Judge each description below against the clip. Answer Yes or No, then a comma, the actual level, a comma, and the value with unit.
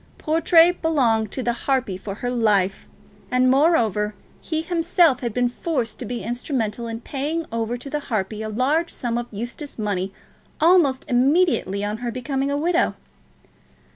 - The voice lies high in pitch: Yes, high, 245 Hz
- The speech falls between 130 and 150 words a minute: No, average, 160 wpm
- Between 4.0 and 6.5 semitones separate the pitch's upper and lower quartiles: Yes, average, 5.3 semitones